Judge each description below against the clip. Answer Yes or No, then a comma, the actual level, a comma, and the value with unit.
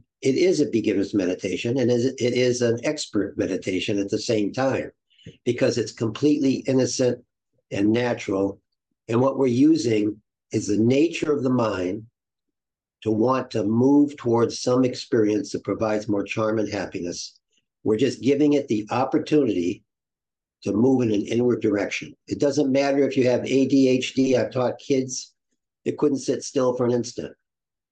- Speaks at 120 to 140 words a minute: No, average, 155 wpm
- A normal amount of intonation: Yes, average, 3.6 semitones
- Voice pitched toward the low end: Yes, low, 125 Hz